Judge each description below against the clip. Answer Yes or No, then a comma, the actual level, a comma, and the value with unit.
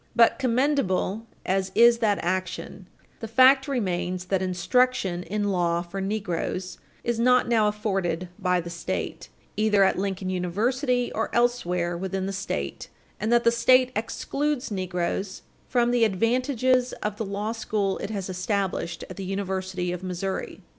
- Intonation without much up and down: No, average, 4.3 semitones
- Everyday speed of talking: Yes, average, 150 wpm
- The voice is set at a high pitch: Yes, high, 200 Hz